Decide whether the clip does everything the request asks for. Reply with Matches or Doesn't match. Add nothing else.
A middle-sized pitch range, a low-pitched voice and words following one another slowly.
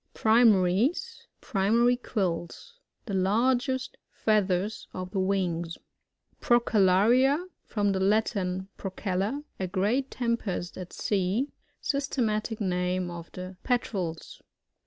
Doesn't match